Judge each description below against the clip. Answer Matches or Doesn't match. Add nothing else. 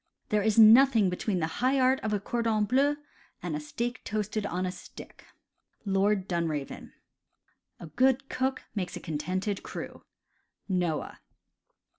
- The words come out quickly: Doesn't match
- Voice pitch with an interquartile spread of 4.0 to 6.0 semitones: Matches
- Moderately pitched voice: Doesn't match